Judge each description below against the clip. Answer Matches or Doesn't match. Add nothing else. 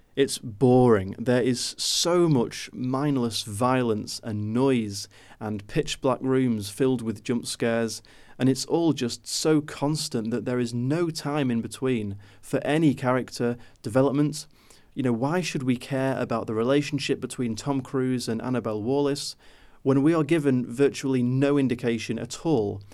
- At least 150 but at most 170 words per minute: Matches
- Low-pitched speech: Matches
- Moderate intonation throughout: Matches